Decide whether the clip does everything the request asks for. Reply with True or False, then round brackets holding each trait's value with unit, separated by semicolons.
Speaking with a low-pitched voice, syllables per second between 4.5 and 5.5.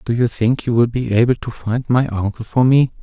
True (115 Hz; 5.2 syllables/s)